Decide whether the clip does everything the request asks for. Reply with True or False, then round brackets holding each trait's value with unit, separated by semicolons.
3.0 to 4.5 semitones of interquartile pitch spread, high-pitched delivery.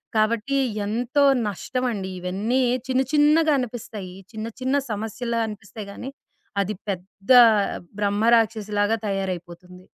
True (3.8 semitones; 215 Hz)